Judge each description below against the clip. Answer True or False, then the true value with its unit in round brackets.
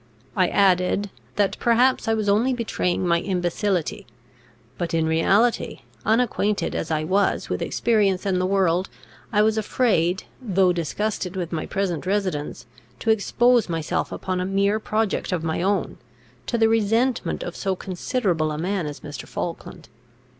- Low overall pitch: False (195 Hz)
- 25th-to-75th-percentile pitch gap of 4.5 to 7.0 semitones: False (3.7 semitones)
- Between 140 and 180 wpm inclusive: True (155 wpm)